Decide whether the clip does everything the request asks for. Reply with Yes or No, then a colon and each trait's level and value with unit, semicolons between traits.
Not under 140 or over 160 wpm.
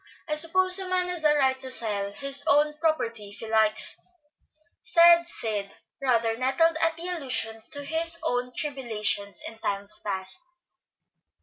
Yes: average, 150 wpm